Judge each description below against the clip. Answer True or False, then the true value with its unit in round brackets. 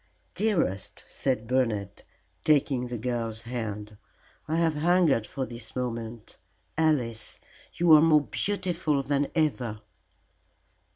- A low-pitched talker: True (130 Hz)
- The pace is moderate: False (110 wpm)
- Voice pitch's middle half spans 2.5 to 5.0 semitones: False (5.4 semitones)